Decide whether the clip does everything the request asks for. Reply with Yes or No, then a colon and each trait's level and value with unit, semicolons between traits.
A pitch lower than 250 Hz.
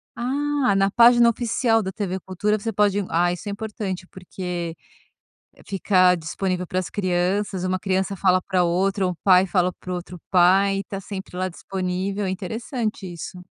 Yes: high, 190 Hz